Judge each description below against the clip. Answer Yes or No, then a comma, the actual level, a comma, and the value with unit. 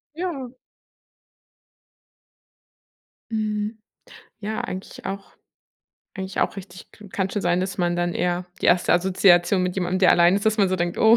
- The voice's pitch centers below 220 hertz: Yes, high, 190 Hz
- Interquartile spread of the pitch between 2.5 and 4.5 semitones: Yes, average, 2.9 semitones